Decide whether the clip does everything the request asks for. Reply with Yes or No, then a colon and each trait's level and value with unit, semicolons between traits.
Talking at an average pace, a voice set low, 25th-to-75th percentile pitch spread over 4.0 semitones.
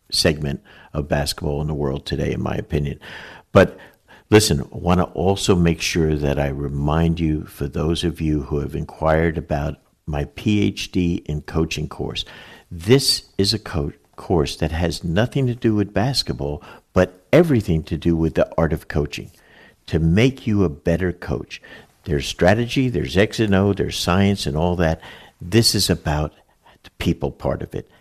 Yes: average, 175 wpm; very low, 85 Hz; average, 4.8 semitones